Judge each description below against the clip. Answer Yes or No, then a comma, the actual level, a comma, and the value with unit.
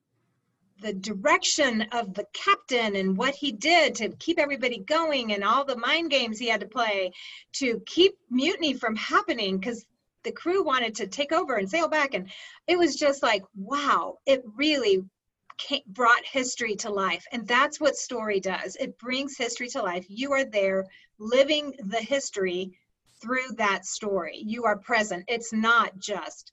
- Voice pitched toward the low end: No, high, 240 Hz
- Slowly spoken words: No, average, 170 wpm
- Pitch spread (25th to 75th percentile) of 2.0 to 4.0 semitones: No, wide, 5.4 semitones